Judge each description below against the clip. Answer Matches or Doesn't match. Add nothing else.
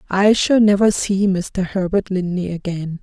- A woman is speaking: Matches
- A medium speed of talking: Matches